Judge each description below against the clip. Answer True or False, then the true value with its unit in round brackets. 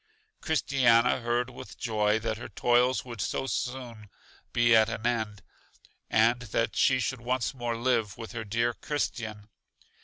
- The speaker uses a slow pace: False (150 wpm)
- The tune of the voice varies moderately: False (2.1 semitones)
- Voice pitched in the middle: False (120 Hz)